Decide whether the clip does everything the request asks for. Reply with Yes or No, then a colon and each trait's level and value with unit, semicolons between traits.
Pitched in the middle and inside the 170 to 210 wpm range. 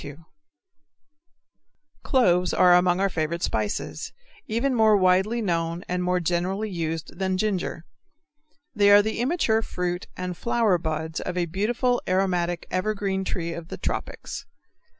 No: medium, 180 Hz; slow, 135 wpm